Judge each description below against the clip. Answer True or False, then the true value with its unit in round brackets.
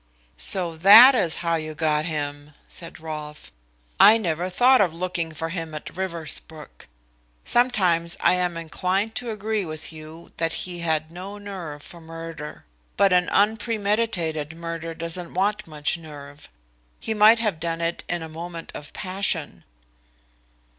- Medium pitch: True (170 Hz)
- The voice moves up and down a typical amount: True (3.6 semitones)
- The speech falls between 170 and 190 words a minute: False (145 wpm)